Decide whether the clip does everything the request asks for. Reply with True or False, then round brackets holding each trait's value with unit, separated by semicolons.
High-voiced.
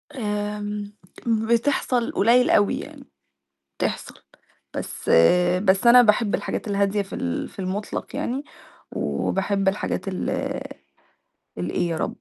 True (205 Hz)